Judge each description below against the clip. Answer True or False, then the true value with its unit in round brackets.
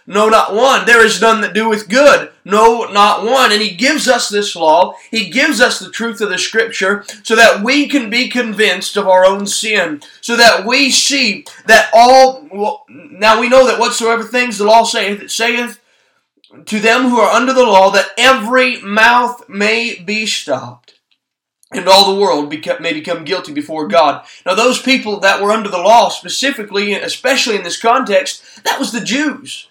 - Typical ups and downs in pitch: True (3.7 semitones)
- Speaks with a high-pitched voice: True (225 Hz)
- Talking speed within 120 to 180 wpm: False (190 wpm)